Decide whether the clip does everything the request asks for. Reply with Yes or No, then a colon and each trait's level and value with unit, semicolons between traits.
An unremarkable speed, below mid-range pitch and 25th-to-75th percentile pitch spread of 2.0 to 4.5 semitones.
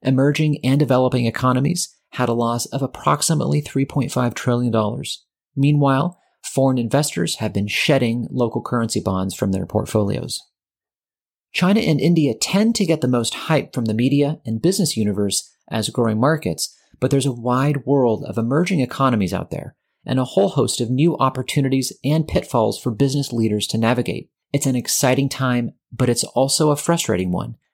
Yes: average, 160 wpm; low, 130 Hz; average, 3.7 semitones